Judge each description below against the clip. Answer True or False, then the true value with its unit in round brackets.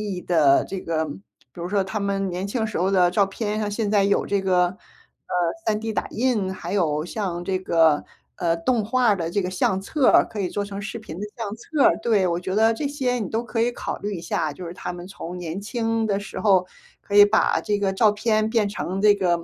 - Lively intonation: False (3.3 semitones)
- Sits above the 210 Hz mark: False (200 Hz)